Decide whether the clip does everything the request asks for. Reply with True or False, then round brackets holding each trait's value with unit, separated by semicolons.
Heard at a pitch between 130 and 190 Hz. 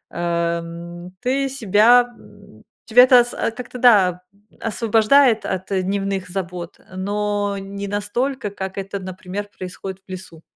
False (200 Hz)